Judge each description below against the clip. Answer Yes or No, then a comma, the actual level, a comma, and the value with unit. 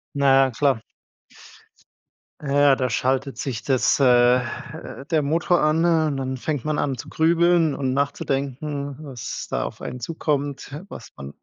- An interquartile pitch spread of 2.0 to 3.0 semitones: Yes, narrow, 2.6 semitones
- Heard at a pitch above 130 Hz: Yes, medium, 140 Hz